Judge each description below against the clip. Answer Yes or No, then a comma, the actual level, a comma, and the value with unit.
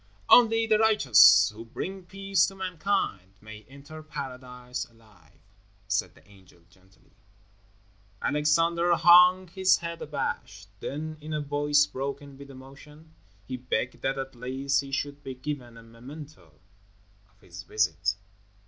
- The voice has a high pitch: No, medium, 140 Hz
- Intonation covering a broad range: Yes, wide, 5.8 semitones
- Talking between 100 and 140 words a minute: Yes, slow, 135 wpm